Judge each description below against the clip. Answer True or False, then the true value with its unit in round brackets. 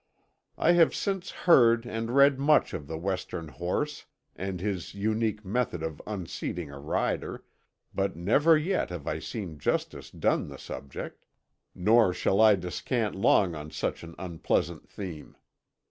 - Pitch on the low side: True (100 Hz)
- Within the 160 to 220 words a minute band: False (145 wpm)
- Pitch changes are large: True (5.7 semitones)